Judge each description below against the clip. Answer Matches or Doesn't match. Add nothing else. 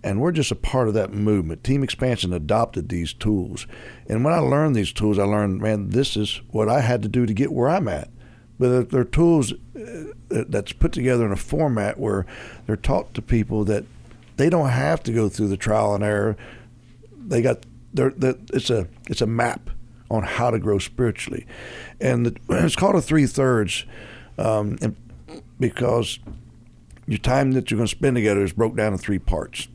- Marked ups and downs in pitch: Doesn't match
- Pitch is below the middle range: Matches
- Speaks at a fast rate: Doesn't match